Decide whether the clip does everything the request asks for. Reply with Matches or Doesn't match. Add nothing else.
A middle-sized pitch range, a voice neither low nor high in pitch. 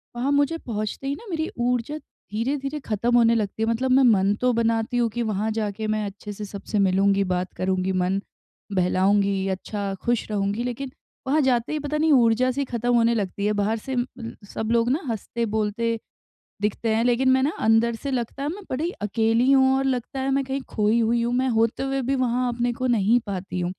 Doesn't match